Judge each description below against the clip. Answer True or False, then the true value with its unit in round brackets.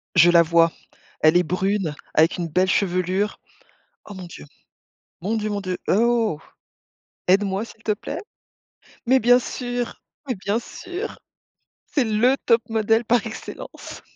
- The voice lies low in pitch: False (205 Hz)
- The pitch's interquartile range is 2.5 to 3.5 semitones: False (4.2 semitones)